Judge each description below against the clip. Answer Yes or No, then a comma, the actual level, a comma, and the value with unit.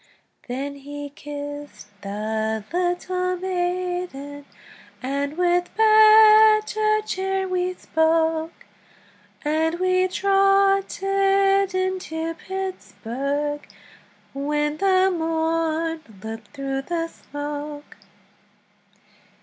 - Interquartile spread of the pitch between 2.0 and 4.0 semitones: No, average, 4.5 semitones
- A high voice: Yes, very high, 330 Hz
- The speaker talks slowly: Yes, slow, 75 wpm